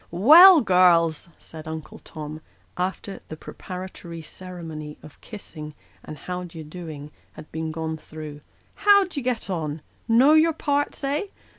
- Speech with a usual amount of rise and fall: No, wide, 6.7 semitones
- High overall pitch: No, medium, 170 Hz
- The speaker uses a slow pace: No, average, 160 wpm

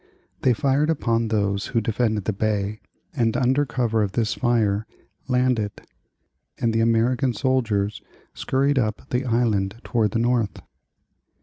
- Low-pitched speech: Yes, low, 115 Hz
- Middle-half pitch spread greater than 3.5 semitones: No, average, 2.8 semitones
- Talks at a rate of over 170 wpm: No, average, 140 wpm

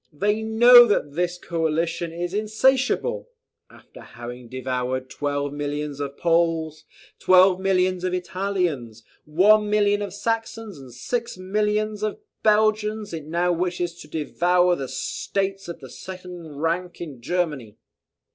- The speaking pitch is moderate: Yes, medium, 180 Hz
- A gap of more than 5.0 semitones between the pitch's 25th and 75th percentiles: Yes, wide, 5.6 semitones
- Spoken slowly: Yes, slow, 130 wpm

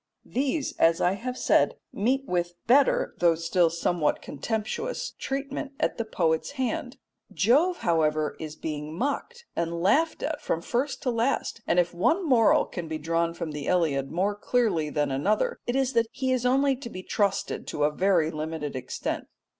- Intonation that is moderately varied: No, wide, 8.1 semitones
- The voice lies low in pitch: No, high, 195 Hz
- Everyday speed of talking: Yes, average, 175 wpm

